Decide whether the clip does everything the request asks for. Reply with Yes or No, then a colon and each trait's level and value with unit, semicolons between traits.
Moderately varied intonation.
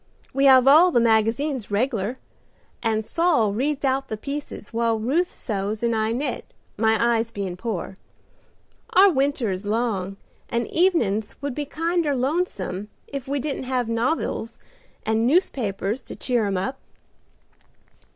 Yes: average, 4.5 semitones